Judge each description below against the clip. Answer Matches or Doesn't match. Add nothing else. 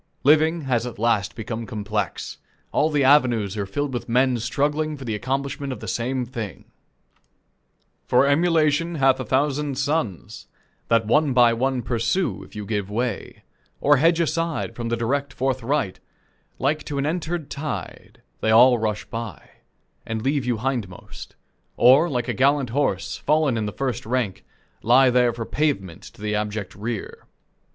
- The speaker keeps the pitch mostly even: Doesn't match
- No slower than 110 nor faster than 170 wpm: Matches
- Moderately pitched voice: Doesn't match